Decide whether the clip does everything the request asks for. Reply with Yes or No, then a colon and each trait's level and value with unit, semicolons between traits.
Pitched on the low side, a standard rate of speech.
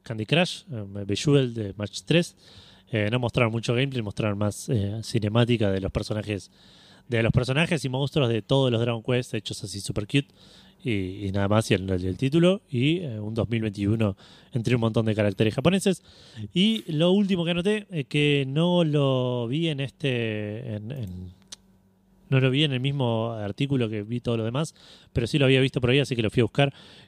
No: low, 120 Hz; fast, 205 wpm